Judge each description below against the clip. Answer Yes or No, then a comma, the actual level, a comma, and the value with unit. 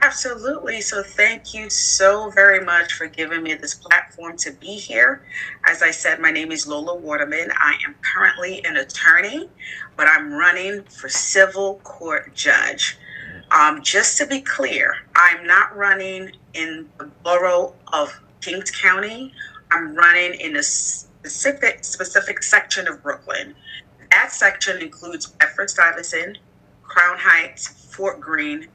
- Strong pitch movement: No, average, 4.4 semitones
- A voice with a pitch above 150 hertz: Yes, high, 190 Hz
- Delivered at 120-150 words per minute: Yes, average, 140 wpm